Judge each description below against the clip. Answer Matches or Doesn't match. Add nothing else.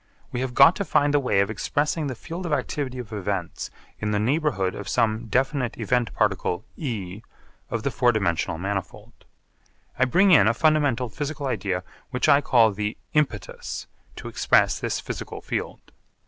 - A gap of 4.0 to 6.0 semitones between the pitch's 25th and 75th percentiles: Matches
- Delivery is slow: Doesn't match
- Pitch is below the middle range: Matches